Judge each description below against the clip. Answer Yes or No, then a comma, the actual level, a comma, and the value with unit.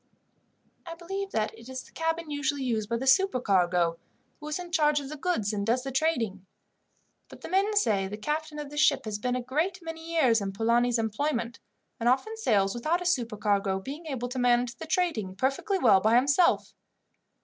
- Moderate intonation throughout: No, wide, 6.4 semitones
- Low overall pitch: No, very high, 260 Hz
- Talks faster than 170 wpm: Yes, average, 195 wpm